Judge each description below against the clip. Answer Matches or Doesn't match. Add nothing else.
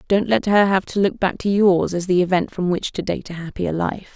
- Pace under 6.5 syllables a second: Matches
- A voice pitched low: Doesn't match